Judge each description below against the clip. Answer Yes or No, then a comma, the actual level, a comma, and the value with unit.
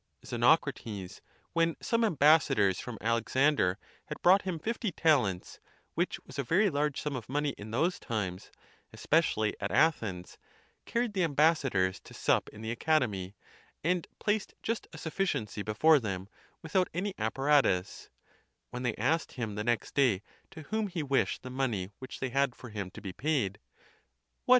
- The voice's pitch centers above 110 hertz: Yes, low, 135 Hz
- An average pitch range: No, wide, 7.3 semitones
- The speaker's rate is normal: Yes, average, 160 wpm